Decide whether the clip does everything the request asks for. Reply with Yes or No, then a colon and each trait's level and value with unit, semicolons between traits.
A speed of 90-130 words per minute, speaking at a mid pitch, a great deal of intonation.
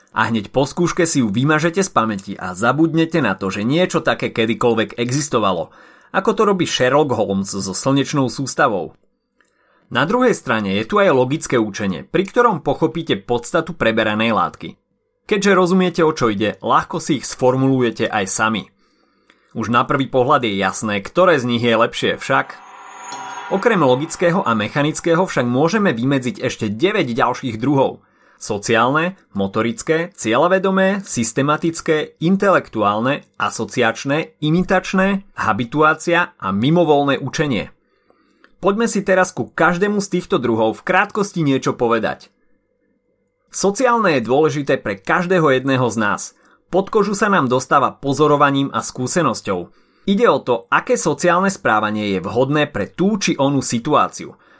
No: average, 140 wpm; medium, 145 Hz; wide, 7.1 semitones